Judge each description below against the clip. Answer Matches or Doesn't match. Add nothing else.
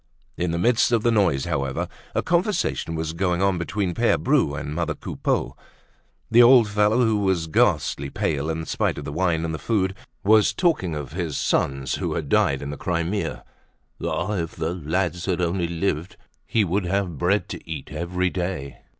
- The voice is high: Doesn't match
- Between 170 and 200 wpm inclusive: Matches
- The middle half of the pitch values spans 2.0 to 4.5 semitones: Matches